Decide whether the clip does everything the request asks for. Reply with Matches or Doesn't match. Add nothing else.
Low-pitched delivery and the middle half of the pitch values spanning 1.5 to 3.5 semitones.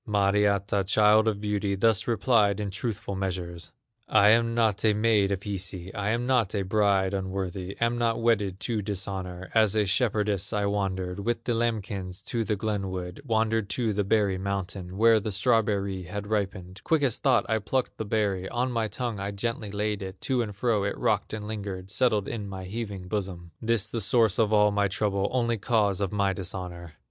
Matches